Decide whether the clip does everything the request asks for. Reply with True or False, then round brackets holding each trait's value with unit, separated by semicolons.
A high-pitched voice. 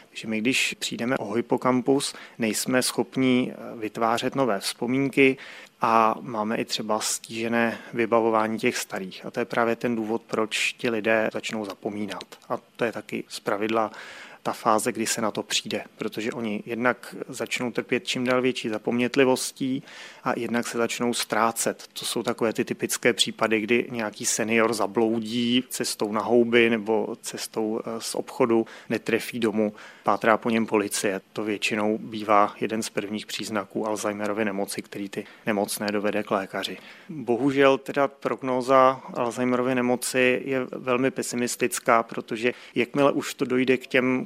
False (115 Hz)